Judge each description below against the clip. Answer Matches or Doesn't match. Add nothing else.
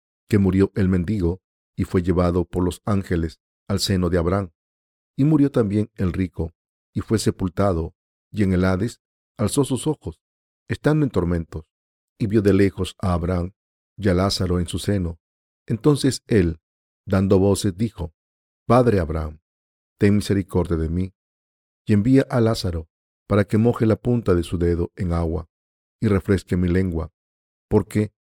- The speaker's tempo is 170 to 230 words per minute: Doesn't match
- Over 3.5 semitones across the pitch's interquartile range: Matches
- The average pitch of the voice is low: Matches